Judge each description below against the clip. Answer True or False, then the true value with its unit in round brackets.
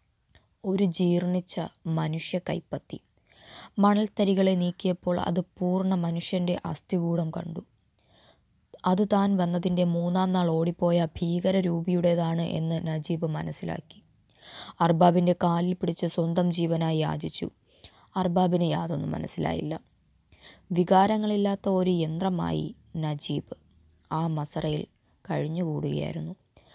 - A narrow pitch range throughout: True (1.9 semitones)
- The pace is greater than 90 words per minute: False (85 wpm)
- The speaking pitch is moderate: True (175 Hz)